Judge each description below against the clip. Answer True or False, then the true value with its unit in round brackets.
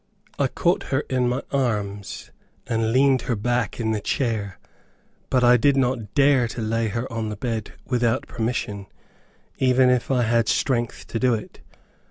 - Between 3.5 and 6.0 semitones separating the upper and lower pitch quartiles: False (2.4 semitones)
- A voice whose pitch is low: True (120 Hz)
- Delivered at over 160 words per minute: True (170 wpm)